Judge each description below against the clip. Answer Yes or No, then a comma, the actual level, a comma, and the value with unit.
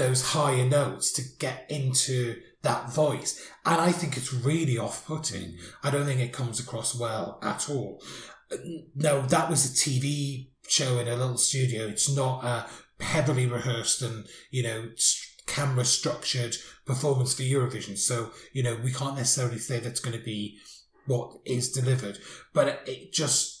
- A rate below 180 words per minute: Yes, average, 160 wpm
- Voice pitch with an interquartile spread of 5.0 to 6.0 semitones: No, average, 3.1 semitones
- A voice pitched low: Yes, low, 130 Hz